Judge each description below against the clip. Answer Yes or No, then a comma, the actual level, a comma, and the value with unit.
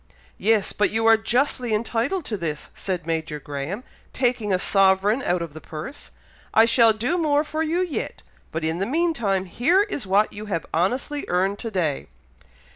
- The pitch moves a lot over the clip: Yes, wide, 5.9 semitones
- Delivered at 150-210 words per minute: Yes, average, 180 wpm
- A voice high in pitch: Yes, high, 215 Hz